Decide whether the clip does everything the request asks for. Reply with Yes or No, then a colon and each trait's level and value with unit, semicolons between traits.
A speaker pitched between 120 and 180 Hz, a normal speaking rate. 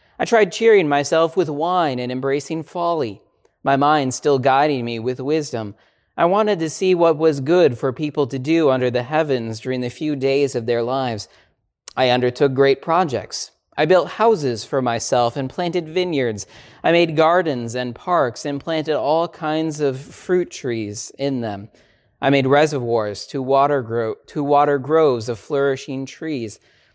Yes: medium, 140 Hz; average, 165 wpm